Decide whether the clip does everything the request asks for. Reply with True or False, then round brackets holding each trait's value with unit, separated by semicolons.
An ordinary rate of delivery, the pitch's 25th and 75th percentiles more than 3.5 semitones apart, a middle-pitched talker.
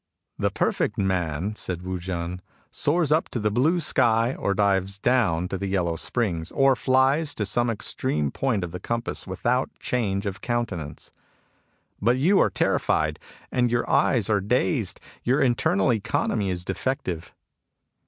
False (160 wpm; 5.2 semitones; 105 Hz)